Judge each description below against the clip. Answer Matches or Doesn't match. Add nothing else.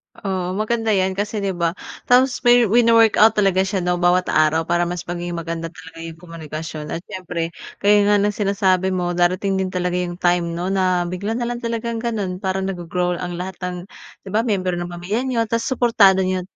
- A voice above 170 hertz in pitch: Matches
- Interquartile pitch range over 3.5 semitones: Doesn't match